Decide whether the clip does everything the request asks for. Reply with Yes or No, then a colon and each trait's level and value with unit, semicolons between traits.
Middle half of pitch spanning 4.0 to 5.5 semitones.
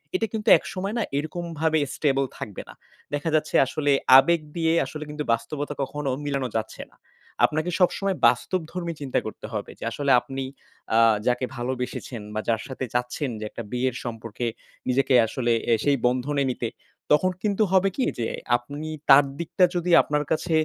Yes: average, 4.7 semitones